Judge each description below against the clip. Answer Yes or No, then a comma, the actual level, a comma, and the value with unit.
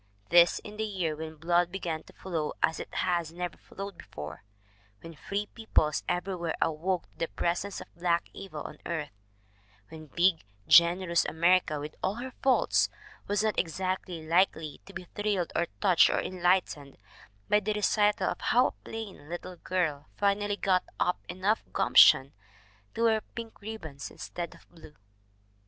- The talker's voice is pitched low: No, medium, 175 Hz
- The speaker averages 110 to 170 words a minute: Yes, average, 160 wpm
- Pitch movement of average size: Yes, average, 3.6 semitones